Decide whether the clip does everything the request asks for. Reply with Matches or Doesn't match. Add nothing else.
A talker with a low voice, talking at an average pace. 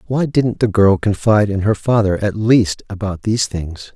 Matches